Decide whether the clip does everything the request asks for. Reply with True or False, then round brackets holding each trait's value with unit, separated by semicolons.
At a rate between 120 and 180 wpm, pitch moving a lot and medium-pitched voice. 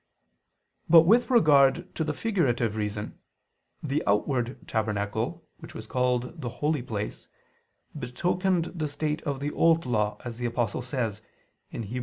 False (140 wpm; 5.8 semitones; 130 Hz)